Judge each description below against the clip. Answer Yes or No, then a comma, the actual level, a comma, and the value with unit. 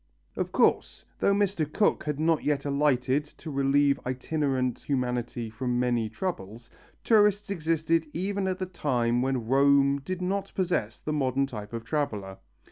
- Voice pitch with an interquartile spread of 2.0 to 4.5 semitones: No, average, 5.1 semitones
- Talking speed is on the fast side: No, average, 150 wpm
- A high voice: No, medium, 140 Hz